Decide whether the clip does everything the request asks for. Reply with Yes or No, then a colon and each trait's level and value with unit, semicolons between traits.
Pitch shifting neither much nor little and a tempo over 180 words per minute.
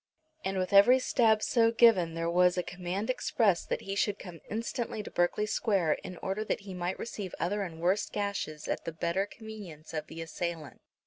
Yes: average, 3.7 semitones; average, 195 wpm